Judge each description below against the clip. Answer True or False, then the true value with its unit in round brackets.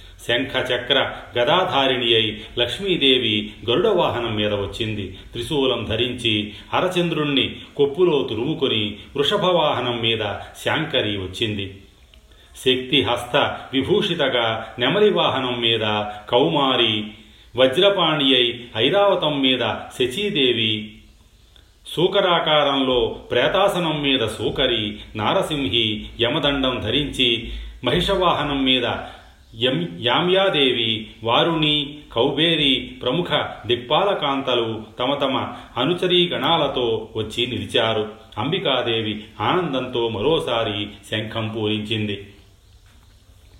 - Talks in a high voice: False (120 Hz)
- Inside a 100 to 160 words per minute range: False (70 wpm)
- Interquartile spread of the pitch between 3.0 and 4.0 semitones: False (4.9 semitones)